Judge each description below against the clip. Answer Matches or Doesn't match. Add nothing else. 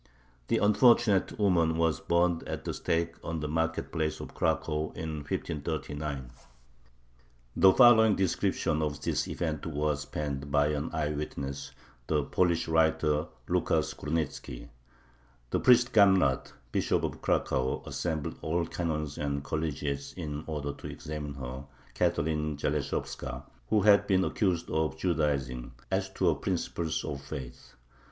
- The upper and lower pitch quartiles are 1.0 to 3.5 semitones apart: Matches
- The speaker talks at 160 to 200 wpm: Doesn't match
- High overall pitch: Doesn't match